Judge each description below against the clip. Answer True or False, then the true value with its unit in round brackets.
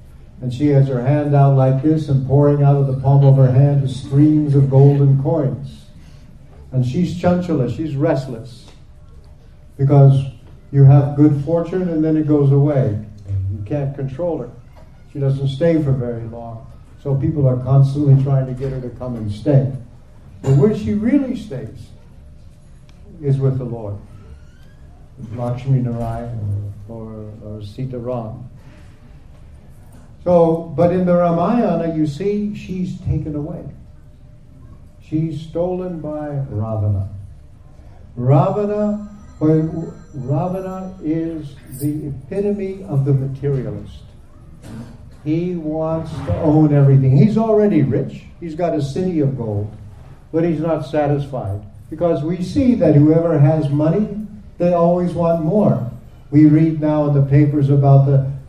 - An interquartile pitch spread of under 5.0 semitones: True (4.5 semitones)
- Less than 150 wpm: True (135 wpm)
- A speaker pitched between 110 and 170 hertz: True (140 Hz)